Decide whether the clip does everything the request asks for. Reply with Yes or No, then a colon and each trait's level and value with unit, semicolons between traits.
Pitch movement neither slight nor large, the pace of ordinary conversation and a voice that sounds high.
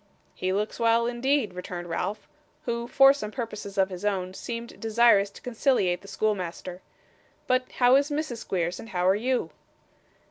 Yes: average, 4.4 semitones; average, 165 wpm; high, 215 Hz